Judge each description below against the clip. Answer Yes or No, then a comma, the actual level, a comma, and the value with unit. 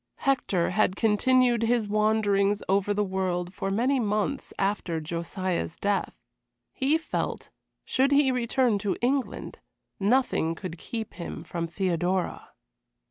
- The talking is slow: Yes, slow, 125 wpm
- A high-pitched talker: Yes, high, 205 Hz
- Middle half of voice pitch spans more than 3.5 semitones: Yes, average, 4.6 semitones